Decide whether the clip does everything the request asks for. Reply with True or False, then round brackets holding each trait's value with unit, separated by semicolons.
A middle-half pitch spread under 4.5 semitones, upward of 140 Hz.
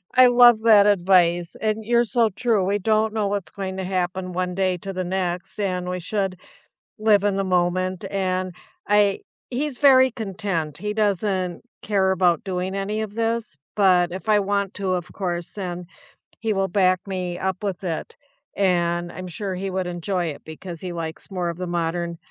True (2.5 semitones; 190 Hz)